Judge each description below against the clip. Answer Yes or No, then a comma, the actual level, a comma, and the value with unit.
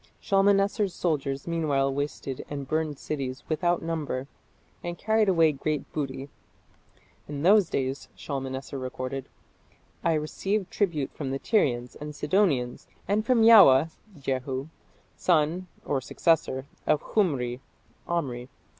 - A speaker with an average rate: No, slow, 115 wpm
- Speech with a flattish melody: No, average, 4.5 semitones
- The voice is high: No, medium, 150 Hz